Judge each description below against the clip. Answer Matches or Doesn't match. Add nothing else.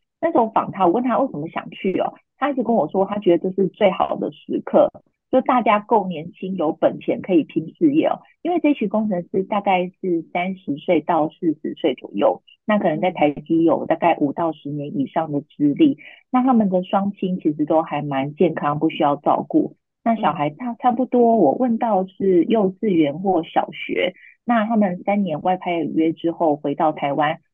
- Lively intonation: Matches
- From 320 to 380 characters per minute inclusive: Doesn't match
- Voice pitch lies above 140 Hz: Matches